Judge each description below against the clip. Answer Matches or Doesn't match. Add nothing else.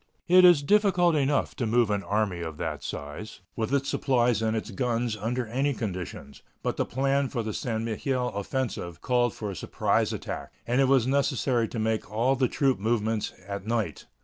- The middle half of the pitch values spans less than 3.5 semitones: Doesn't match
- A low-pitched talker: Matches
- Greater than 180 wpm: Matches